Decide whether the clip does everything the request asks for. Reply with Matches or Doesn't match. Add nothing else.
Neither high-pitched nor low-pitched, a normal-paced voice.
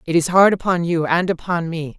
Doesn't match